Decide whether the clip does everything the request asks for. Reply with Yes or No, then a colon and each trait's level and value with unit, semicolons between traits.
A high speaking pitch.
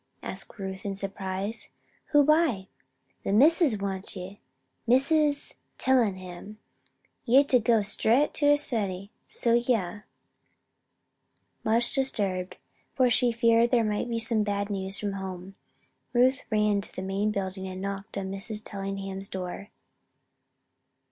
Yes: high, 205 Hz